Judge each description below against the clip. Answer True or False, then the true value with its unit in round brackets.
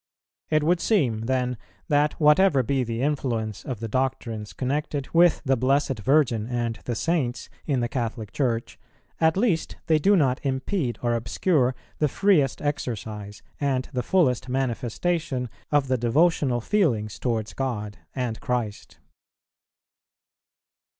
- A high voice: False (130 Hz)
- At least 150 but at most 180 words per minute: False (135 wpm)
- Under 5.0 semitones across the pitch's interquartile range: True (4.2 semitones)